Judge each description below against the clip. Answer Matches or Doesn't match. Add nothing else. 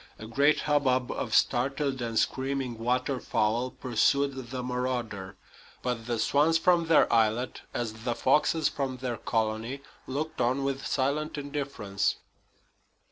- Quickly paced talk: Doesn't match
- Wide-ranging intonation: Doesn't match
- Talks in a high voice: Doesn't match